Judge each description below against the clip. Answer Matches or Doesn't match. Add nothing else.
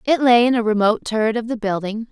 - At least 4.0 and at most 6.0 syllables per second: Doesn't match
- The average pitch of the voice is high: Matches